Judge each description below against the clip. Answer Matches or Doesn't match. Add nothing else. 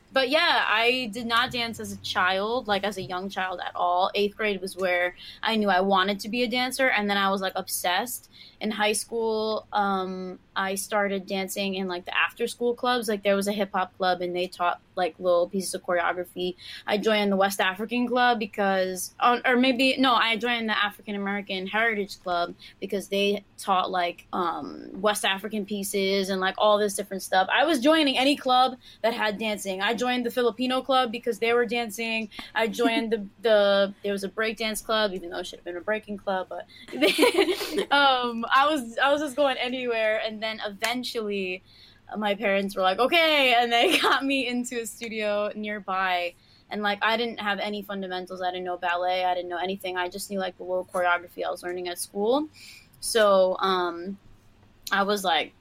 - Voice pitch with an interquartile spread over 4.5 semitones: Doesn't match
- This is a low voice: Doesn't match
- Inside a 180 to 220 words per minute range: Matches